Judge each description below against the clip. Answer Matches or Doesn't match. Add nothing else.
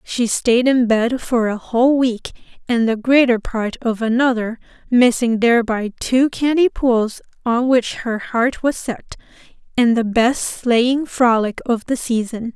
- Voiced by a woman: Matches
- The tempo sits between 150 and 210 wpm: Matches